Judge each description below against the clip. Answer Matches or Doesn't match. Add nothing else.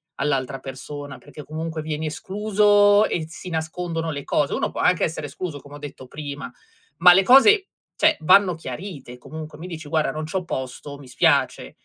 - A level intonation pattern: Doesn't match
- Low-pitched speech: Doesn't match